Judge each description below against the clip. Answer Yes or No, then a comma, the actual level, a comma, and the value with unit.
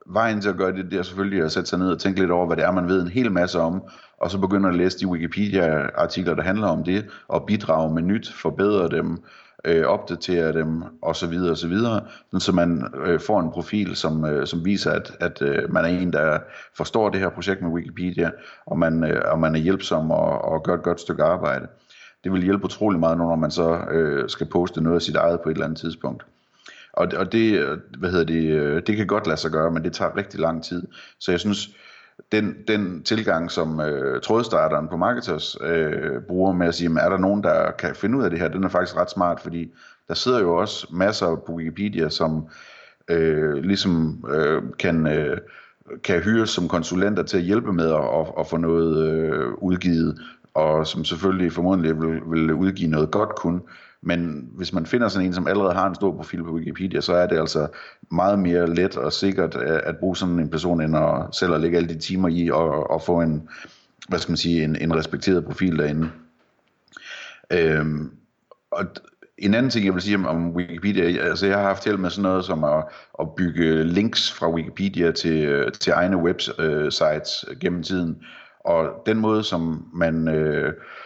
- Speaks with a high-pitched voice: No, very low, 85 Hz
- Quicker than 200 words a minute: Yes, average, 210 wpm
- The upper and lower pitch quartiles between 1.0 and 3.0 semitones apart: Yes, average, 2.7 semitones